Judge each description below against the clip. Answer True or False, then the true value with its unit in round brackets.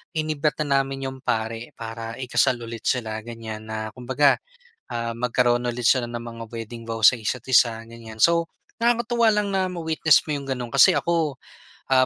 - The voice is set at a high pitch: False (125 Hz)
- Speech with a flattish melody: False (4.0 semitones)